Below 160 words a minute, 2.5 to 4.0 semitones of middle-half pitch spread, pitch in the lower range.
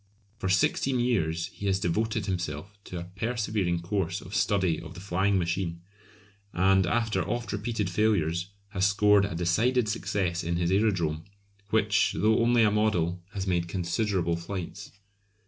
Yes: average, 150 wpm; average, 3.6 semitones; very low, 95 Hz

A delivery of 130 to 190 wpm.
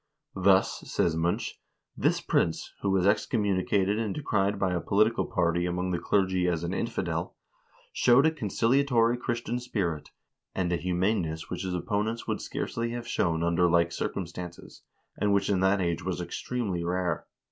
Yes: average, 160 wpm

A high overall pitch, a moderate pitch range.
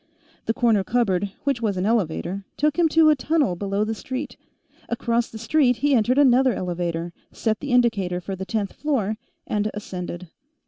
Yes: high, 220 Hz; average, 5.0 semitones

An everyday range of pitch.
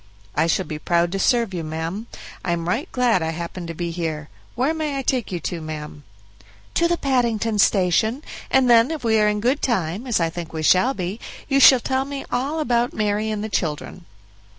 No: wide, 6.7 semitones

